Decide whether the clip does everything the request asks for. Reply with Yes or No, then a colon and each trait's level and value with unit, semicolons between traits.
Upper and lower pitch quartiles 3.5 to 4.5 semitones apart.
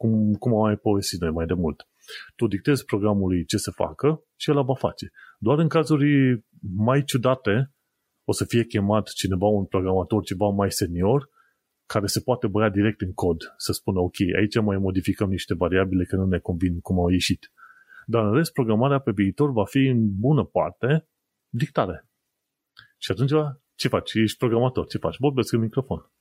No: average, 5.1 semitones